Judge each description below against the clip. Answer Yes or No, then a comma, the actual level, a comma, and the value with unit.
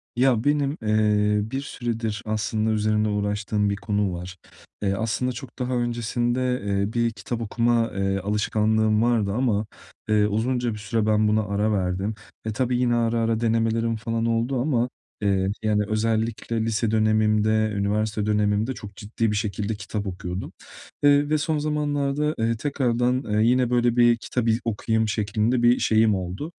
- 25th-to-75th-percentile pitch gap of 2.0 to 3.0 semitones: Yes, narrow, 2.4 semitones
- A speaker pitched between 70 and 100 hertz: No, low, 110 Hz